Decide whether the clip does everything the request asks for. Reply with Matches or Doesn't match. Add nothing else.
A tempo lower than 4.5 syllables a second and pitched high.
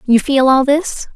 Matches